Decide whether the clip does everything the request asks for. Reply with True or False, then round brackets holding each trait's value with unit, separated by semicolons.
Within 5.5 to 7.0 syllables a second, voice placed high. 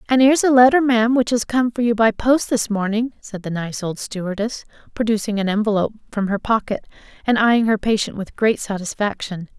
True (5.9 syllables/s; 220 Hz)